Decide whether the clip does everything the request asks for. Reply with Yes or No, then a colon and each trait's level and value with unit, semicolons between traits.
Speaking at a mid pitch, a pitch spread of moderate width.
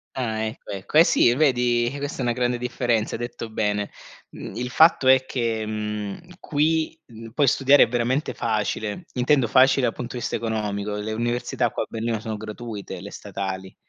No: low, 120 Hz; average, 3.1 semitones